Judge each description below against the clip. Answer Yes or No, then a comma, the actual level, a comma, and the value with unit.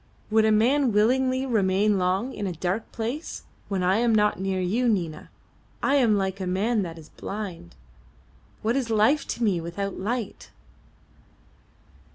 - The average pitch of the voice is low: No, high, 210 Hz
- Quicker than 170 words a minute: No, average, 160 wpm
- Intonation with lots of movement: No, average, 3.9 semitones